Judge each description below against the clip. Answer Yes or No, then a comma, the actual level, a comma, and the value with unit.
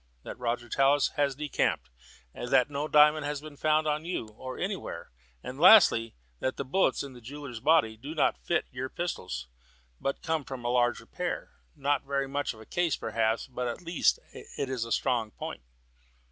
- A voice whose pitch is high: No, low, 135 Hz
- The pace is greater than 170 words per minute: Yes, average, 180 wpm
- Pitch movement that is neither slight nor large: Yes, average, 3.8 semitones